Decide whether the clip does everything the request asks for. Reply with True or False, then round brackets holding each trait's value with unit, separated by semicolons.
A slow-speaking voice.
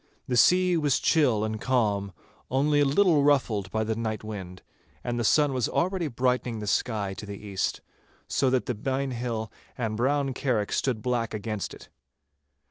False (175 wpm)